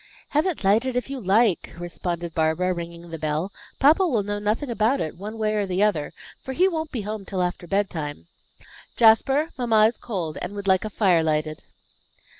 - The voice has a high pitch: Yes, high, 205 Hz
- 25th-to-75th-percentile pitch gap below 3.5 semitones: No, average, 5.1 semitones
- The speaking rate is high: No, average, 195 wpm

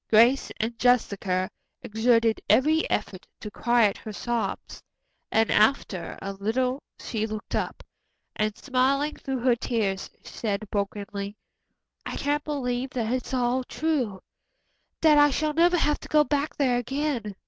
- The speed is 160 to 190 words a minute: No, average, 140 wpm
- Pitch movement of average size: Yes, average, 4.5 semitones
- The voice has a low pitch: No, high, 245 Hz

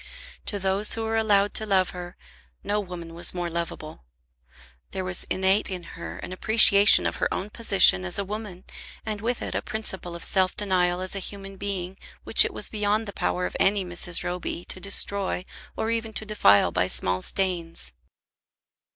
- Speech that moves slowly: No, average, 185 wpm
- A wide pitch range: No, average, 2.8 semitones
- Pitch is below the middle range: No, high, 190 Hz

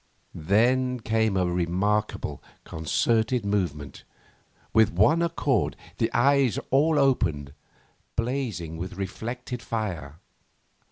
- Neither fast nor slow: No, slow, 95 wpm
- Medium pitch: No, low, 110 Hz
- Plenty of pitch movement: Yes, wide, 6.3 semitones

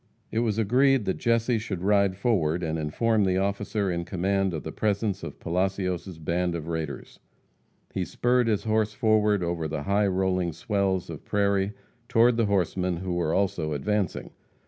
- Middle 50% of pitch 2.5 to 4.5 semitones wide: Yes, average, 3.4 semitones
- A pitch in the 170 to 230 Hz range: No, very low, 95 Hz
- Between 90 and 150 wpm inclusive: No, average, 170 wpm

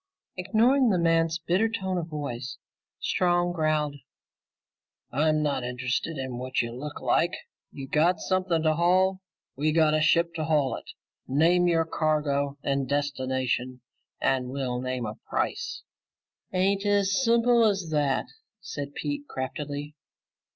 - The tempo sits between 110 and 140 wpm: Yes, slow, 135 wpm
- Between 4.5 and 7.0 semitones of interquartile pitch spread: Yes, average, 4.8 semitones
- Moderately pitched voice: Yes, medium, 155 Hz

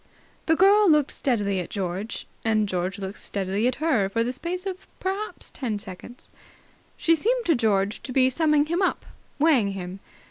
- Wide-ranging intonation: Yes, wide, 8.6 semitones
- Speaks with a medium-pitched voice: No, high, 245 Hz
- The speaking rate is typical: Yes, average, 175 wpm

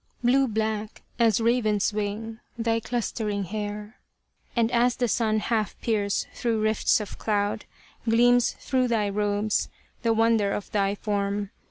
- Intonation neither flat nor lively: No, narrow, 2.0 semitones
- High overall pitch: Yes, high, 220 Hz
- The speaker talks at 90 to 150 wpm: Yes, average, 140 wpm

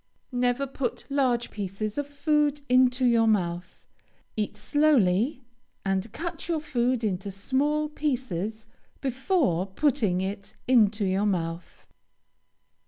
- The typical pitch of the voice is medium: No, high, 240 Hz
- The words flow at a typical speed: No, slow, 110 wpm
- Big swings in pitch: Yes, wide, 6.0 semitones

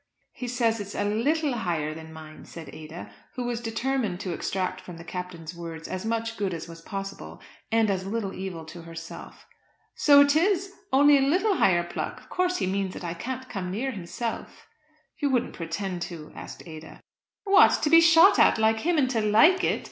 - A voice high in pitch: Yes, high, 205 Hz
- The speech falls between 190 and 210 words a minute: Yes, average, 200 wpm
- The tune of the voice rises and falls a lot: Yes, wide, 7.4 semitones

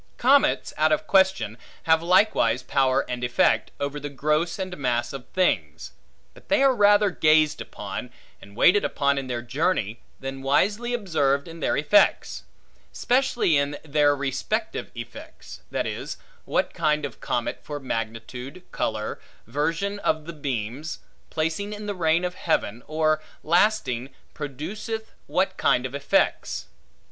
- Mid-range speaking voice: Yes, medium, 150 Hz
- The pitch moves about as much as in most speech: No, wide, 5.7 semitones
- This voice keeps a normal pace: Yes, average, 145 wpm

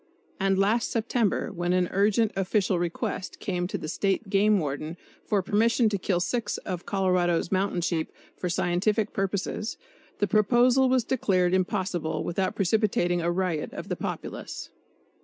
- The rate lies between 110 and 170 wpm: Yes, average, 150 wpm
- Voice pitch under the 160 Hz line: No, high, 190 Hz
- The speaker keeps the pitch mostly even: No, average, 3.1 semitones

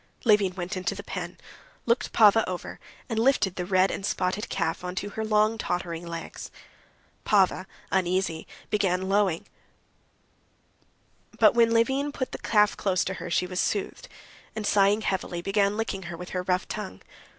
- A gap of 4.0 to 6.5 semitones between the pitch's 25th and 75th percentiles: No, average, 2.7 semitones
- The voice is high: Yes, high, 195 Hz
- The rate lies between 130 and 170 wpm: Yes, average, 160 wpm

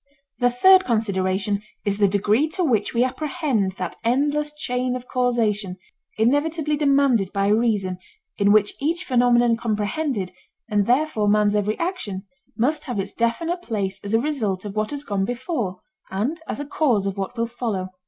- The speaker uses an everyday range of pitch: No, wide, 5.7 semitones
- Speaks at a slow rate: No, average, 165 wpm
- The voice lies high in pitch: Yes, high, 230 Hz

